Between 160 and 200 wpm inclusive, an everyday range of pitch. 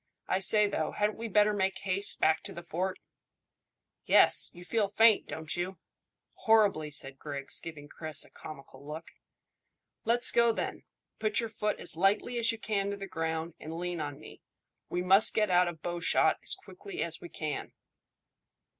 Yes: average, 175 wpm; average, 4.7 semitones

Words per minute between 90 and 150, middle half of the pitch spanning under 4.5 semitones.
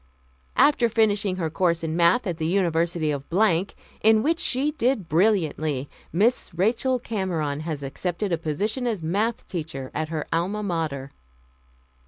No: average, 145 wpm; wide, 5.5 semitones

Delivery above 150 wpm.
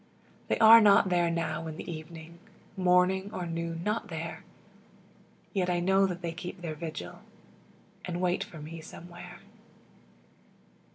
No: average, 140 wpm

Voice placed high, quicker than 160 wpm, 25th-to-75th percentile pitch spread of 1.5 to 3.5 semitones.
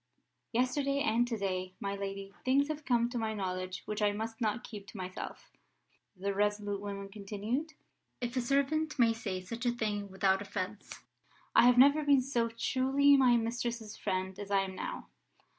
No: high, 225 Hz; average, 175 wpm; average, 4.1 semitones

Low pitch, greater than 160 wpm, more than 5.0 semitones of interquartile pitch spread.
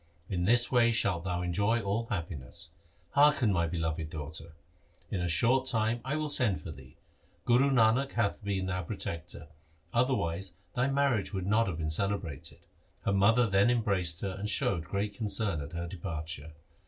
Yes: low, 100 Hz; average, 170 wpm; wide, 5.6 semitones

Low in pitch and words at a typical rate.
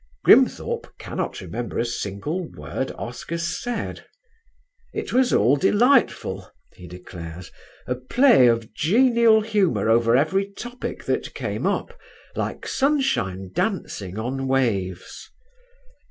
No: low, 130 Hz; slow, 110 wpm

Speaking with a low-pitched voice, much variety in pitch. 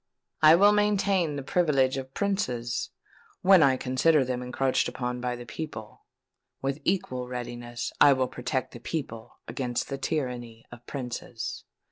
No: low, 130 Hz; average, 4.1 semitones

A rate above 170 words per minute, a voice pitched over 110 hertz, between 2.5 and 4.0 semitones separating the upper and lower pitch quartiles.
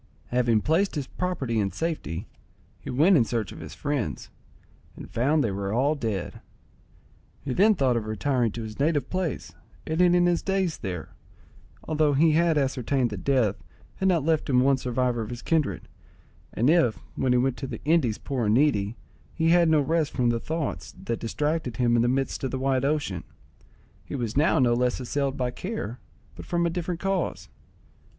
No: average, 190 wpm; low, 135 Hz; average, 5.2 semitones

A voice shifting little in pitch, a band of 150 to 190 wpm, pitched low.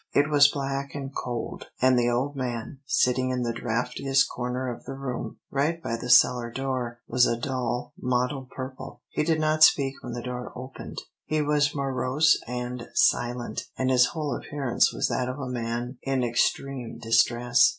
Yes: narrow, 2.0 semitones; average, 175 wpm; low, 130 Hz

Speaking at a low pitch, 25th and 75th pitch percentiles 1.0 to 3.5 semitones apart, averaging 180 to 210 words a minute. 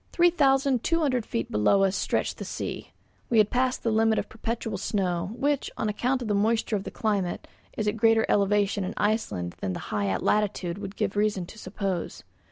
No: high, 210 Hz; average, 3.1 semitones; fast, 205 wpm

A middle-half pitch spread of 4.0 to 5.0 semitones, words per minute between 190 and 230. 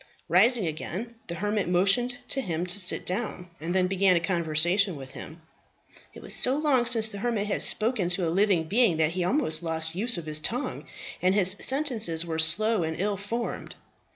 Yes: average, 4.7 semitones; fast, 205 wpm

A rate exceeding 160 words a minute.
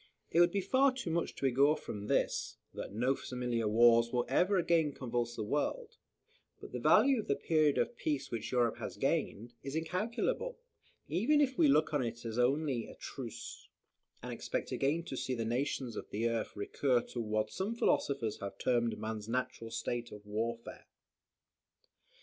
Yes: average, 175 wpm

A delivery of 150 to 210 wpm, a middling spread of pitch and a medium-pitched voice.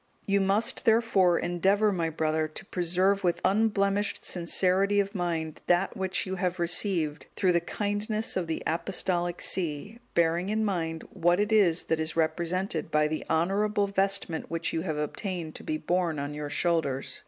Yes: average, 165 wpm; average, 3.4 semitones; medium, 180 Hz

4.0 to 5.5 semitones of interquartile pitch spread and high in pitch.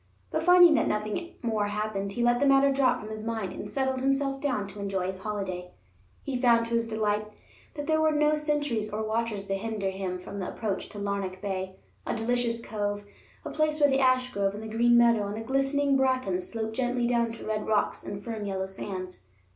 Yes: average, 4.4 semitones; high, 220 Hz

